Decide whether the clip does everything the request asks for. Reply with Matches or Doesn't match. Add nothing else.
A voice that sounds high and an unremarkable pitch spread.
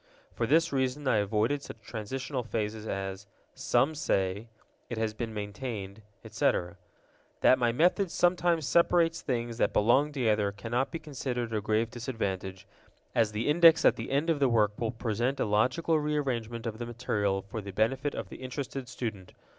Doesn't match